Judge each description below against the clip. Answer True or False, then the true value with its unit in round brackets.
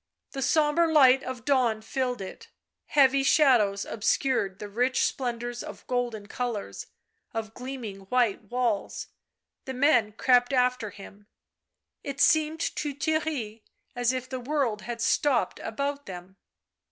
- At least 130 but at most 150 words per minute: True (135 wpm)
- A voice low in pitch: False (250 Hz)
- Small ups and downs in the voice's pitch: False (3.9 semitones)